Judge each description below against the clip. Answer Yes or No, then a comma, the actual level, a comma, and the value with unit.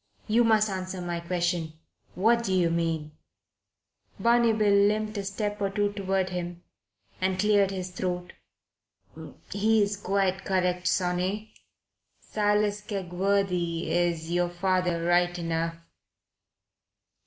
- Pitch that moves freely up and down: No, average, 2.7 semitones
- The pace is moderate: No, slow, 110 wpm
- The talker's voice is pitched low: No, medium, 185 Hz